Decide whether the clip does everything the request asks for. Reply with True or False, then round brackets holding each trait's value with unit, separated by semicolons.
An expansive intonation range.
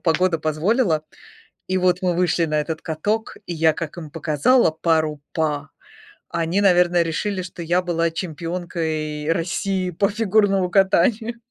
False (2.8 semitones)